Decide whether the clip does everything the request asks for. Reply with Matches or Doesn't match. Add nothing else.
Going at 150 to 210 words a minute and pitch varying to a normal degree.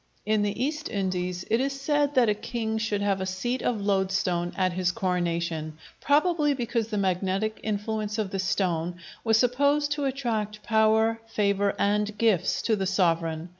Matches